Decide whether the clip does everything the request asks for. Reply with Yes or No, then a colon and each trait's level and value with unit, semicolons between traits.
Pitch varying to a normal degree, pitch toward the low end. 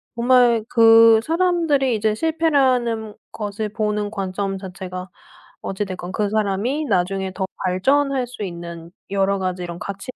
No: average, 4.6 semitones; high, 210 Hz